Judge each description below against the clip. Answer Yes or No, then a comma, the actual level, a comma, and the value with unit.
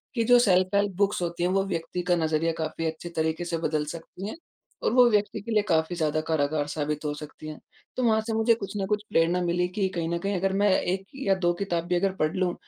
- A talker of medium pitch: Yes, medium, 175 Hz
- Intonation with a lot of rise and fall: No, average, 3.7 semitones